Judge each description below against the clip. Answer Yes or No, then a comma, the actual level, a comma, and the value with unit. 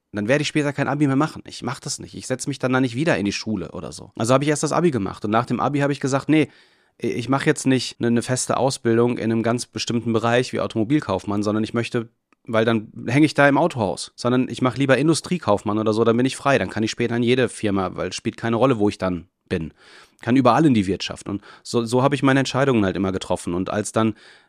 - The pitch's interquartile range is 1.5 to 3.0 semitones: No, average, 3.9 semitones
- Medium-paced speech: No, fast, 260 wpm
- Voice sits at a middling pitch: No, low, 120 Hz